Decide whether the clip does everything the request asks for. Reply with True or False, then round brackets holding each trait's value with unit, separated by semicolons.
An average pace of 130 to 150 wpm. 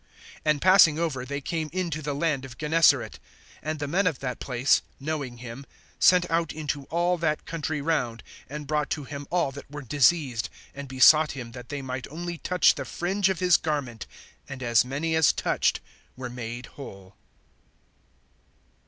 False (170 wpm)